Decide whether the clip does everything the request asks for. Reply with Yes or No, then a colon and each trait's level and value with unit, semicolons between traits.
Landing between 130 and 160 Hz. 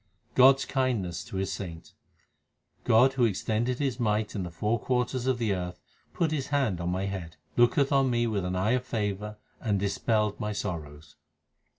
No: low, 105 Hz